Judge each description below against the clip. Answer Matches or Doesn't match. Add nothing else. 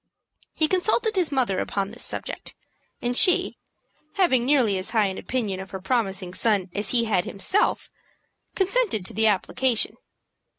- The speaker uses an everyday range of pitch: Doesn't match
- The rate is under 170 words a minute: Matches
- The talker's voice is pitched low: Doesn't match